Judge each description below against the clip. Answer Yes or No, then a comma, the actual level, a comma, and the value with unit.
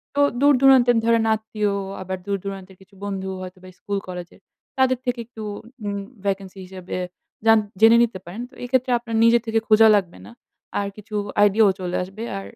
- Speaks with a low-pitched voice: No, high, 210 Hz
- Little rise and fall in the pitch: No, average, 3.4 semitones